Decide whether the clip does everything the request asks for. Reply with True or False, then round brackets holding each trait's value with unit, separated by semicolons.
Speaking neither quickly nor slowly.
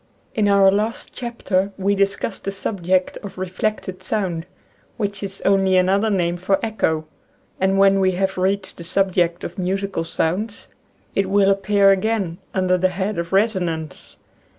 True (155 wpm)